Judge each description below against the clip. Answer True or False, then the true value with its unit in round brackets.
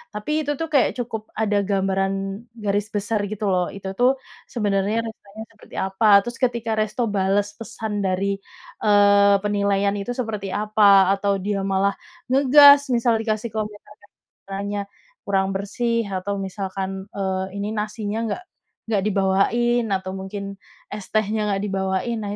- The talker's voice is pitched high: True (205 Hz)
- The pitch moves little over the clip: True (2.1 semitones)